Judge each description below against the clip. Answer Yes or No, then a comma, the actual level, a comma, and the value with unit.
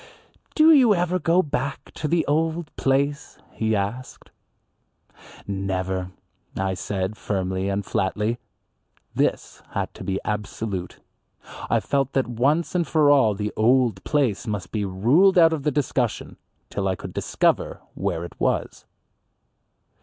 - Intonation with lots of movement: Yes, wide, 7.3 semitones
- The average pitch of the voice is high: No, low, 115 Hz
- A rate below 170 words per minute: Yes, average, 140 wpm